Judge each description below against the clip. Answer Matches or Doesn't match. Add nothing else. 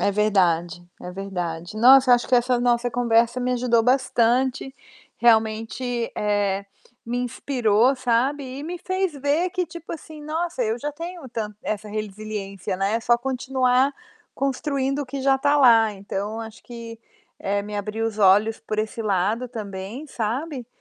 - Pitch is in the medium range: Doesn't match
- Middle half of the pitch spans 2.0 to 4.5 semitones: Matches